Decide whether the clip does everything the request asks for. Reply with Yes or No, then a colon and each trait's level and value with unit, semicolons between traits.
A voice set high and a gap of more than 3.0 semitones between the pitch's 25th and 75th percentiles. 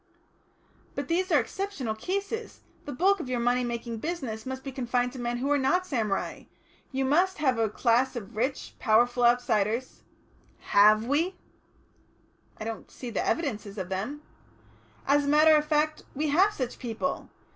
Yes: very high, 260 Hz; average, 4.6 semitones